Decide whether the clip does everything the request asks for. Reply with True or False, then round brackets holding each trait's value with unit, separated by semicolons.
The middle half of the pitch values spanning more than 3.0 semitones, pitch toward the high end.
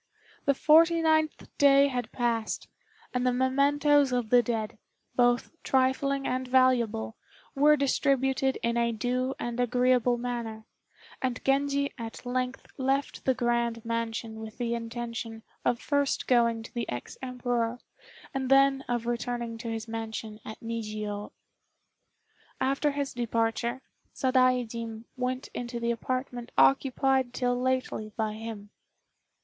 False (2.4 semitones; 245 Hz)